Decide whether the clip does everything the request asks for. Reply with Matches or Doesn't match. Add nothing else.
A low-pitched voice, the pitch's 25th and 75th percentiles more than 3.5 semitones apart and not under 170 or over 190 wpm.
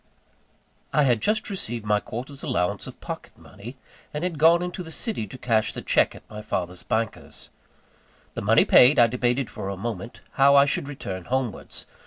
Matches